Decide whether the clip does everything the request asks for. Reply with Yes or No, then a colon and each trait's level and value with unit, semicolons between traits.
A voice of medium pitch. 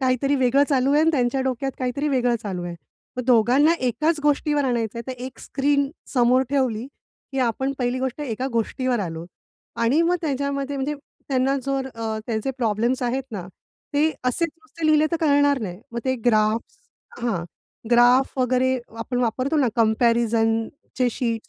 No: very high, 255 Hz